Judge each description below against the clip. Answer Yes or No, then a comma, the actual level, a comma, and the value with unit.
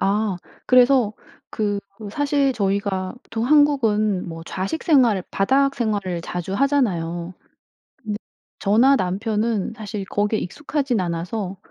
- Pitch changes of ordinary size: Yes, average, 5.0 semitones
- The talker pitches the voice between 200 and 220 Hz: Yes, high, 210 Hz